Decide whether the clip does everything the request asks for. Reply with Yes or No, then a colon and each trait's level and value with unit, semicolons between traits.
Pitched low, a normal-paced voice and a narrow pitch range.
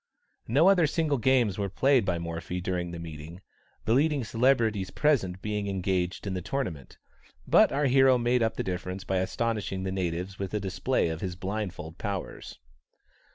No: low, 100 Hz; average, 170 wpm; wide, 5.5 semitones